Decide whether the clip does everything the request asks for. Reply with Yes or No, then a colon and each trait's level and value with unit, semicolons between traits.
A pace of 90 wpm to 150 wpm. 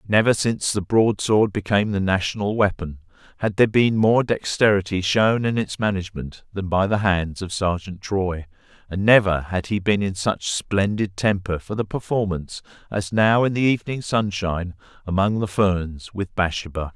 No: average, 165 wpm